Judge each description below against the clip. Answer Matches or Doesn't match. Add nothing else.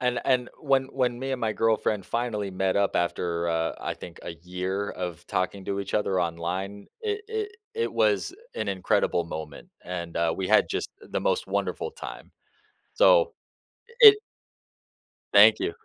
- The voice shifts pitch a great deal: Matches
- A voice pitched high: Doesn't match